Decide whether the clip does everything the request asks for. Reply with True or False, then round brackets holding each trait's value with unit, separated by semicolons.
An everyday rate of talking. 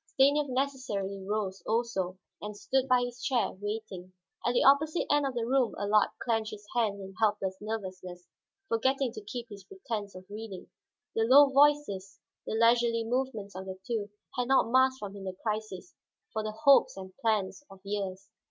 True (175 wpm)